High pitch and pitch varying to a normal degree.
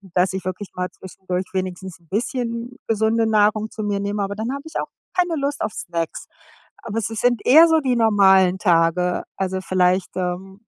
Yes: high, 200 Hz; average, 3.6 semitones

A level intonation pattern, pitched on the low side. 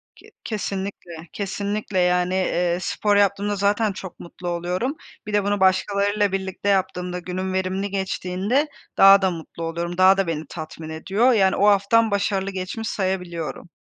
No: narrow, 2.1 semitones; high, 190 Hz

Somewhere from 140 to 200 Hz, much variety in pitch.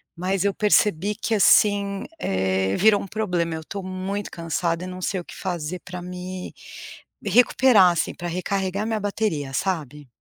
No: medium, 185 Hz; average, 3.1 semitones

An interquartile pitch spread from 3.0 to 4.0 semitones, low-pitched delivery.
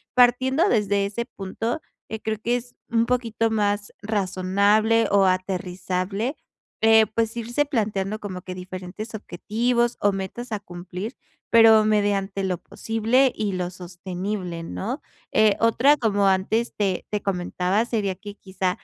No: average, 3.3 semitones; high, 205 Hz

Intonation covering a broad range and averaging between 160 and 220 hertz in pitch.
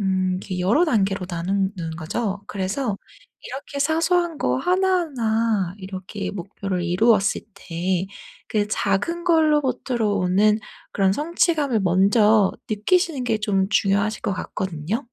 Yes: wide, 5.7 semitones; high, 205 Hz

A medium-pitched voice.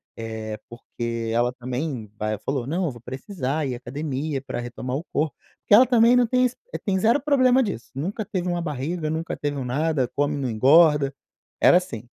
Yes: medium, 145 Hz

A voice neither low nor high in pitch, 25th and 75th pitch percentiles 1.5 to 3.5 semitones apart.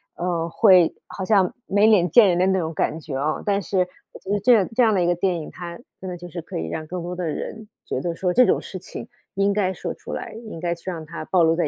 Yes: medium, 180 Hz; average, 2.8 semitones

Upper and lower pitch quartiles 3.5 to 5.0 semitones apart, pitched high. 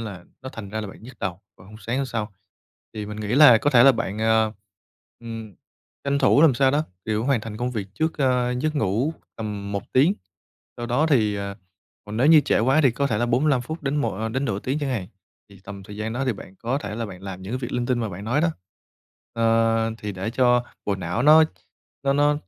No: average, 4.3 semitones; low, 115 Hz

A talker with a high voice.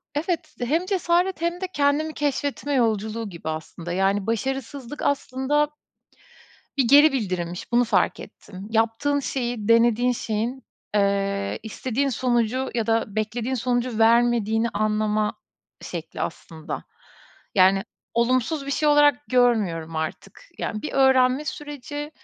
Yes: high, 240 Hz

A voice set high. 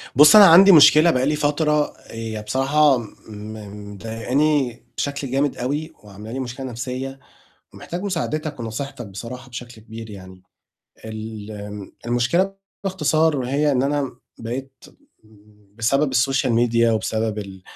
No: low, 130 Hz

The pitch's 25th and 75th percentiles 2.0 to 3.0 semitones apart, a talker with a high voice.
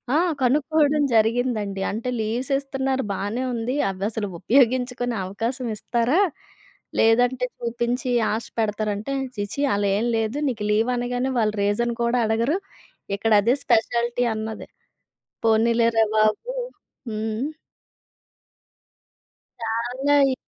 Yes: narrow, 2.5 semitones; high, 235 Hz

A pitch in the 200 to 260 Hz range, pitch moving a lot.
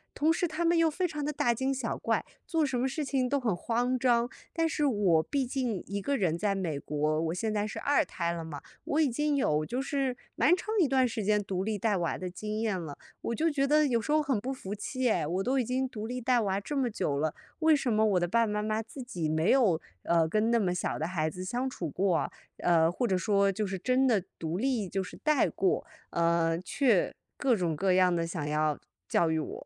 Yes: high, 215 Hz; wide, 6.9 semitones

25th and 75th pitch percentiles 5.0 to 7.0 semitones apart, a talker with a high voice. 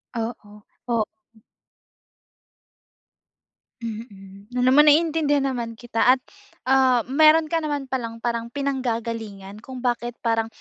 No: average, 3.2 semitones; high, 240 Hz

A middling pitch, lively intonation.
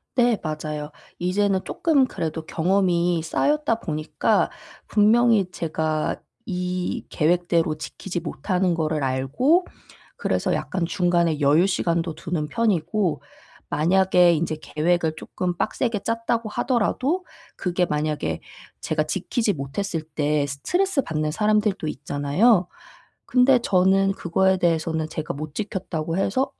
No: medium, 175 Hz; average, 4.8 semitones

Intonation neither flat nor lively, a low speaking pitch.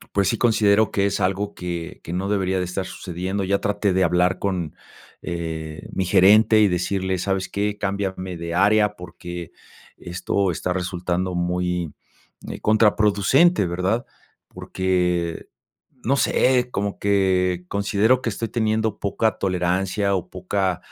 No: narrow, 2.3 semitones; very low, 95 Hz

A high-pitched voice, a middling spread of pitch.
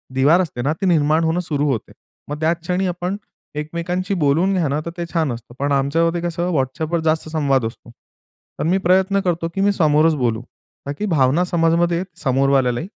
No: medium, 160 Hz; average, 3.7 semitones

